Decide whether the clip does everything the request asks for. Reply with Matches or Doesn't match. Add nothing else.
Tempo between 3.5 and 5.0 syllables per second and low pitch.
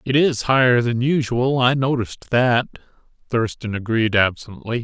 Matches